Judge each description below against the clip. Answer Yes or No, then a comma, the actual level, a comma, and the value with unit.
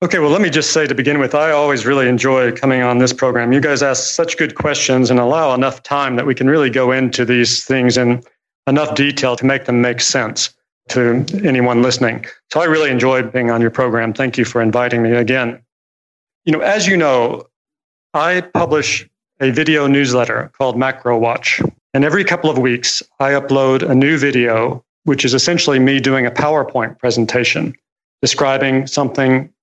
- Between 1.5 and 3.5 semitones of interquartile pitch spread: Yes, average, 2.9 semitones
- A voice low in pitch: Yes, low, 130 Hz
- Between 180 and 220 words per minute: Yes, average, 190 wpm